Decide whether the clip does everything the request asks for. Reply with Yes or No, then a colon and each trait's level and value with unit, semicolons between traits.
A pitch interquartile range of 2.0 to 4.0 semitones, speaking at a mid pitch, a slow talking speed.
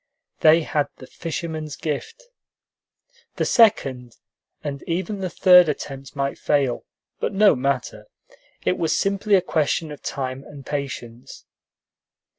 No: average, 4.6 semitones; medium, 150 Hz; slow, 125 wpm